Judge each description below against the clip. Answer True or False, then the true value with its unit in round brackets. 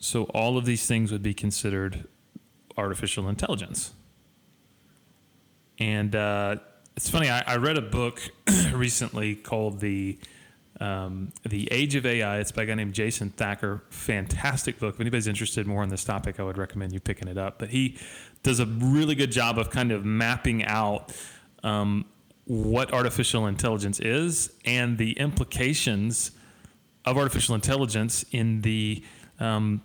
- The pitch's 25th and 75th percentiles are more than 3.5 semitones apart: False (3.1 semitones)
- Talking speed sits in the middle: True (155 wpm)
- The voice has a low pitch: True (110 Hz)